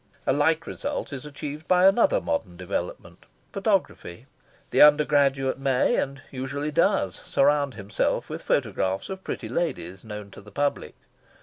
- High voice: No, medium, 140 Hz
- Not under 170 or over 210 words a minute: No, average, 140 wpm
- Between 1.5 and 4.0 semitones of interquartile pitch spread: No, average, 4.4 semitones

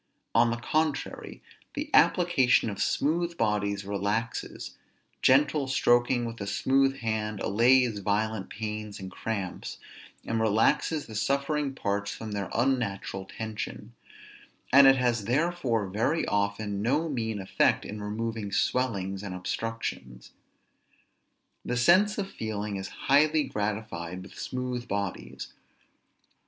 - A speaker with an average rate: No, slow, 120 wpm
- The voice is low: Yes, low, 110 Hz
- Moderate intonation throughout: Yes, average, 4.6 semitones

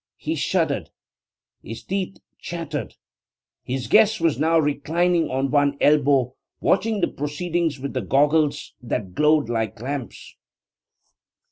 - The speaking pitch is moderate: Yes, medium, 145 Hz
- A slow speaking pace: Yes, slow, 120 wpm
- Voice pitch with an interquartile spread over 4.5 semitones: No, average, 4.1 semitones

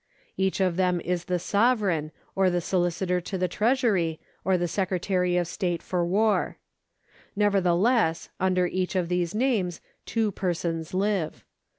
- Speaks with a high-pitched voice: No, medium, 180 Hz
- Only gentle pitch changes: Yes, narrow, 2.3 semitones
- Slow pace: No, average, 145 wpm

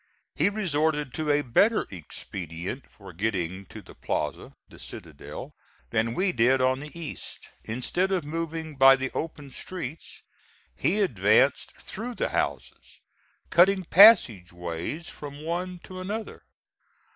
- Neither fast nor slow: No, slow, 130 wpm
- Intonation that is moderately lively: No, wide, 7.8 semitones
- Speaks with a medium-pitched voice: Yes, medium, 145 Hz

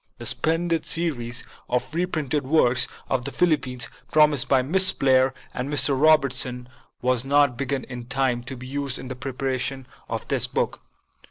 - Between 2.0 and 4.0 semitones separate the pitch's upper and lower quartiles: Yes, average, 2.8 semitones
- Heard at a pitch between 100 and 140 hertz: Yes, low, 135 Hz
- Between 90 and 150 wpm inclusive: No, average, 160 wpm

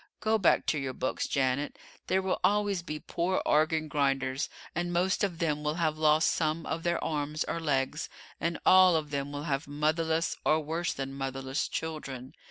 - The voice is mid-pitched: Yes, medium, 155 Hz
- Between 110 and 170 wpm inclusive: No, average, 180 wpm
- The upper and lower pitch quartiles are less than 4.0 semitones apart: Yes, average, 3.0 semitones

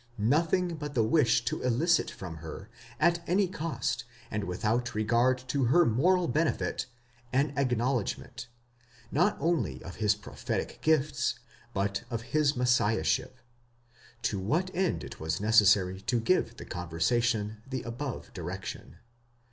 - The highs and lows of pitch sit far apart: Yes, wide, 6.2 semitones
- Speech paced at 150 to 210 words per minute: No, slow, 135 wpm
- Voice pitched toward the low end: Yes, low, 120 Hz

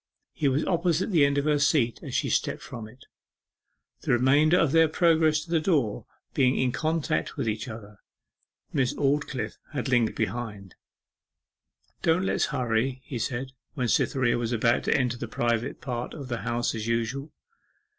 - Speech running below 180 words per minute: Yes, average, 170 wpm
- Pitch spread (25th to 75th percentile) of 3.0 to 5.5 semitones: Yes, average, 4.2 semitones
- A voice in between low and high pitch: No, low, 130 Hz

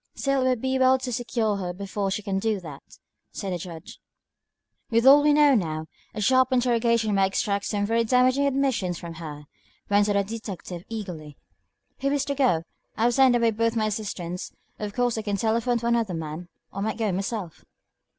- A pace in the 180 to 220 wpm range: Yes, average, 200 wpm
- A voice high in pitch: Yes, high, 220 Hz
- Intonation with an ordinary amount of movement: Yes, average, 4.3 semitones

